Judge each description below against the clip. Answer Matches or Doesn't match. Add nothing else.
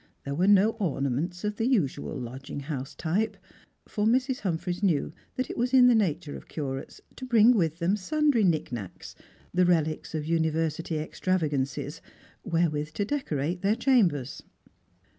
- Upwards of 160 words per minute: Doesn't match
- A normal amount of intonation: Doesn't match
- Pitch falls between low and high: Matches